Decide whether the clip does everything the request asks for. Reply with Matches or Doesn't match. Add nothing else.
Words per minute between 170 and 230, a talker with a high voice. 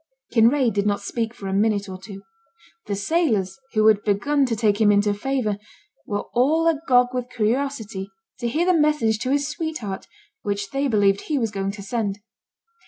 Matches